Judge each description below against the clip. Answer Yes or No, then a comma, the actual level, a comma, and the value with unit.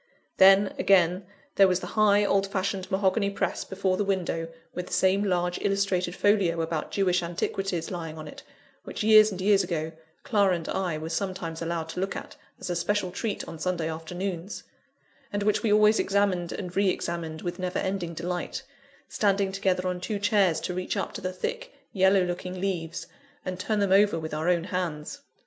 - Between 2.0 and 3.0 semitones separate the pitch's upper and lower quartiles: Yes, narrow, 2.4 semitones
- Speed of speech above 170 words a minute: Yes, average, 190 wpm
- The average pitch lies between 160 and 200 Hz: Yes, medium, 185 Hz